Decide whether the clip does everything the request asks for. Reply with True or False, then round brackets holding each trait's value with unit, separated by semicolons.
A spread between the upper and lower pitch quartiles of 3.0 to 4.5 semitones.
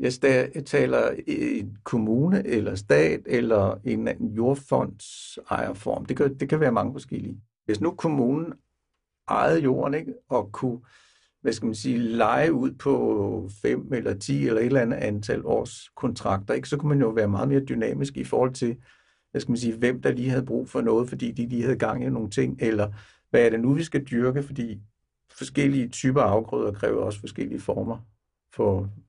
True (3.9 semitones)